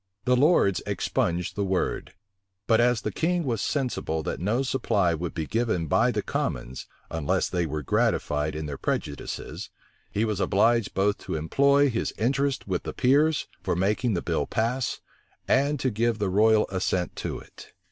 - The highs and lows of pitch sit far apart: Yes, wide, 6.3 semitones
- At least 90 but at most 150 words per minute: No, average, 170 wpm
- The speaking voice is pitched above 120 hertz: No, low, 105 Hz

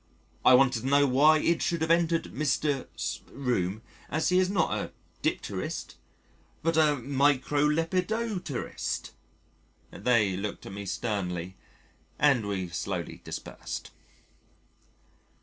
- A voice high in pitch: No, medium, 140 Hz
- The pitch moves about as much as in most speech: No, wide, 7.3 semitones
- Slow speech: Yes, slow, 115 wpm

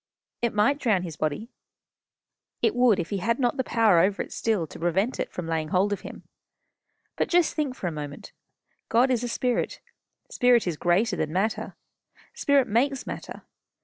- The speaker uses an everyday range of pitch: No, wide, 6.0 semitones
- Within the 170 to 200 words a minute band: Yes, average, 180 wpm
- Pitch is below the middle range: No, high, 215 Hz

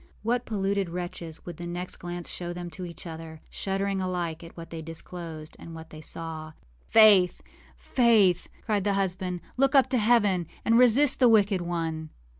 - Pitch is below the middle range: No, medium, 180 Hz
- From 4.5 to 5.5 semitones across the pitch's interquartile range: No, average, 3.7 semitones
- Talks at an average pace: Yes, average, 175 wpm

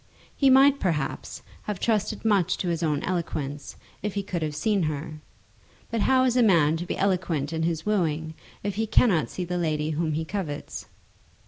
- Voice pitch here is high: No, medium, 175 Hz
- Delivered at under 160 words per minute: No, average, 190 wpm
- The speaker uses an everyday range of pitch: Yes, average, 4.9 semitones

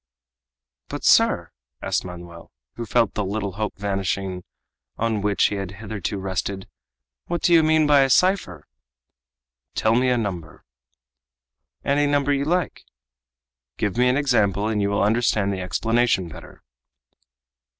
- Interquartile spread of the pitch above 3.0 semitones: Yes, average, 4.9 semitones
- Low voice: Yes, low, 105 Hz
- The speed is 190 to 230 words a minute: No, average, 140 wpm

